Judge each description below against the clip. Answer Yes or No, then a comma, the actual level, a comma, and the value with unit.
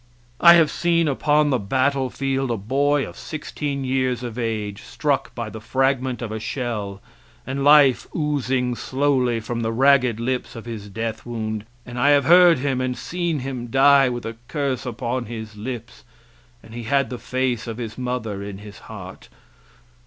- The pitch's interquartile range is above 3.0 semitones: Yes, average, 3.4 semitones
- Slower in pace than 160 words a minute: No, average, 170 wpm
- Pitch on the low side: Yes, low, 125 Hz